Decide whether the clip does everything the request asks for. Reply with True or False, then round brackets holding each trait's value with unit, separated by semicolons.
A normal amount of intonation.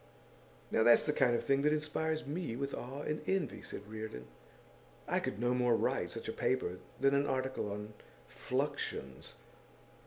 True (4.8 semitones)